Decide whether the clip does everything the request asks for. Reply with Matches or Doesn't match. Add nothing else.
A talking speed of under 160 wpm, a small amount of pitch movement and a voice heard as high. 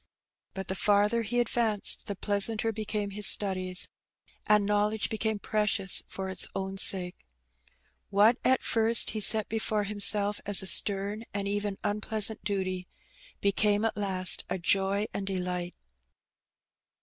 Matches